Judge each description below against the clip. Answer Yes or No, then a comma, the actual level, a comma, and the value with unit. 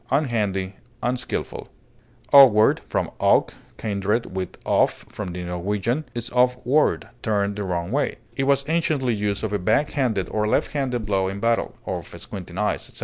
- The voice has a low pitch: Yes, low, 110 Hz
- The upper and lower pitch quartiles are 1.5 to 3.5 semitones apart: No, average, 4.3 semitones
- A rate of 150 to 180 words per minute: Yes, average, 170 wpm